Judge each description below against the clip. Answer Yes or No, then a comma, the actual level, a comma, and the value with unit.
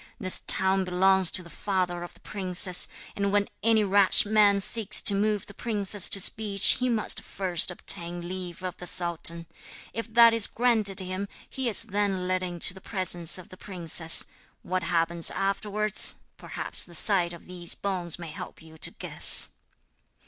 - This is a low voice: No, high, 190 Hz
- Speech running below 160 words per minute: No, average, 170 wpm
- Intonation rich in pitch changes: No, narrow, 2.6 semitones